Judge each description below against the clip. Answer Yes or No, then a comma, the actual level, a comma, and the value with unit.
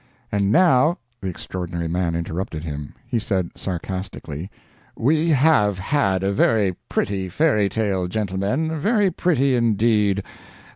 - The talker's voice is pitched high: No, low, 100 Hz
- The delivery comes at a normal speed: No, slow, 130 wpm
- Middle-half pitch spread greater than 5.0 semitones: Yes, wide, 5.6 semitones